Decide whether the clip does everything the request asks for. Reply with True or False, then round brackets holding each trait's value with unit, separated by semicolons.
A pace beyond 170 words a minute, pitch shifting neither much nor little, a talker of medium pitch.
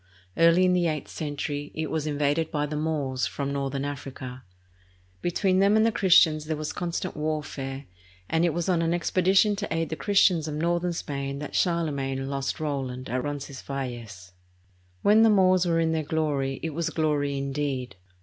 True (180 wpm; 3.5 semitones; 155 Hz)